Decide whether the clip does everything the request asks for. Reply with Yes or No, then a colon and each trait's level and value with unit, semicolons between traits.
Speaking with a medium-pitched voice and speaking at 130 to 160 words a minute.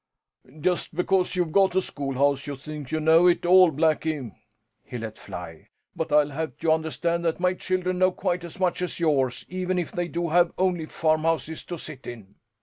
No: medium, 165 Hz; average, 190 wpm